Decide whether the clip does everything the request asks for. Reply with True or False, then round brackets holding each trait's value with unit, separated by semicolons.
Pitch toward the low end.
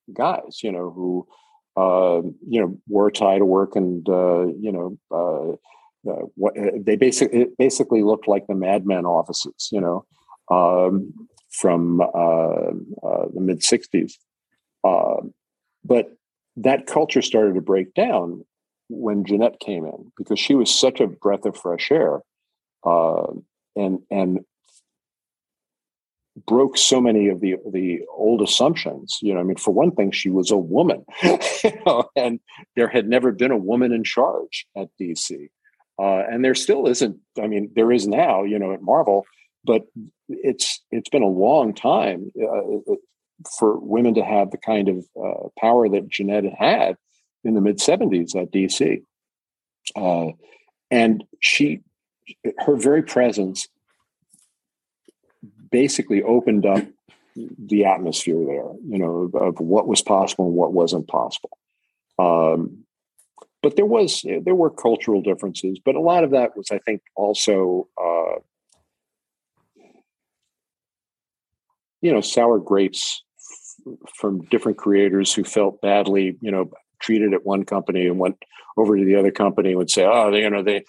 True (100 Hz)